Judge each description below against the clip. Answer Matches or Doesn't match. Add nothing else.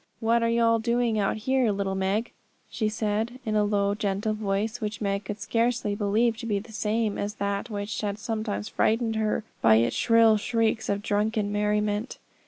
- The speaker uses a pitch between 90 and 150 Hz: Doesn't match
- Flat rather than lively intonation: Matches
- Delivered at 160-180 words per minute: Doesn't match